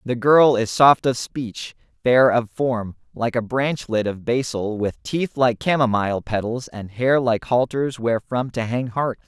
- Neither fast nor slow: Yes, average, 175 wpm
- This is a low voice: Yes, low, 120 Hz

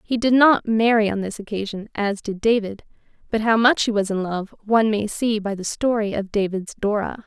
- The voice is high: Yes, high, 215 Hz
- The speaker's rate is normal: No, fast, 215 wpm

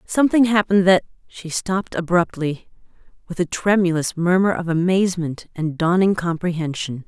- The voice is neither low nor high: Yes, medium, 175 Hz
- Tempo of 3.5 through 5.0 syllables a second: No, 5.3 syllables/s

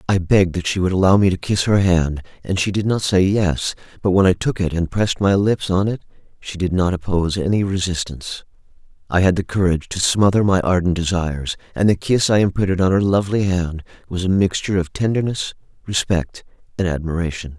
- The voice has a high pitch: No, very low, 95 Hz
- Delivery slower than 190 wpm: No, fast, 205 wpm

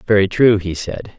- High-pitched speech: No, low, 100 Hz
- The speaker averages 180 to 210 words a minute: Yes, fast, 205 wpm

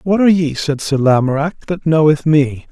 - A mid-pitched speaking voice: Yes, medium, 155 Hz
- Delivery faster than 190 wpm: Yes, average, 200 wpm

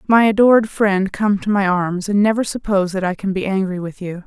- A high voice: Yes, high, 195 Hz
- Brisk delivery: Yes, fast, 240 wpm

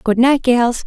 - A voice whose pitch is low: No, high, 245 Hz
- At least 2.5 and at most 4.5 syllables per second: Yes, 4.0 syllables/s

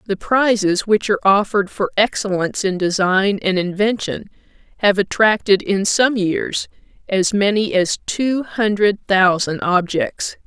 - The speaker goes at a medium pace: No, slow, 130 wpm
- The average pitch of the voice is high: Yes, high, 200 Hz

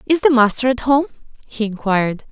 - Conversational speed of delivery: Yes, average, 180 wpm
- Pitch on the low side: No, high, 245 Hz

